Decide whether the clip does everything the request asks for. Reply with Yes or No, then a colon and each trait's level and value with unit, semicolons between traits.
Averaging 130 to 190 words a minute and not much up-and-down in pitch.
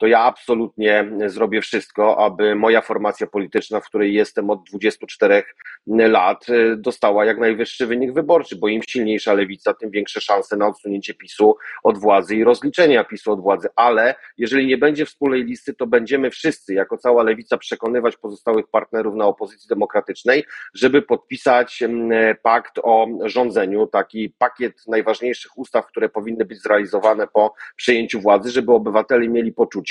Yes: average, 150 wpm; narrow, 2.2 semitones